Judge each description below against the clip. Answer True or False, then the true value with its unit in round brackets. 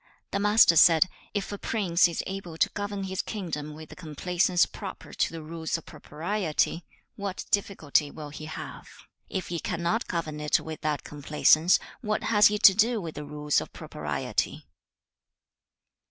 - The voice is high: False (170 Hz)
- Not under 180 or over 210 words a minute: False (165 wpm)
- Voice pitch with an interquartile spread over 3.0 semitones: True (4.4 semitones)